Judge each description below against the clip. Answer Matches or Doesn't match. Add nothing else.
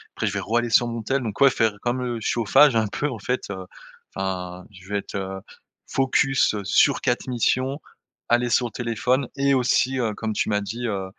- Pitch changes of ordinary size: Matches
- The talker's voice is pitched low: Matches